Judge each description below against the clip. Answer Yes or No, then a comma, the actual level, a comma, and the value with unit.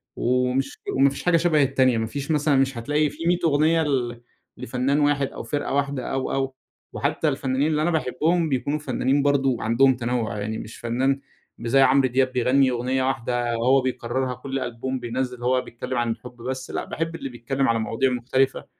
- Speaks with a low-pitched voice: Yes, low, 130 Hz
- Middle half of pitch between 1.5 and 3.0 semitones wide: Yes, narrow, 2.4 semitones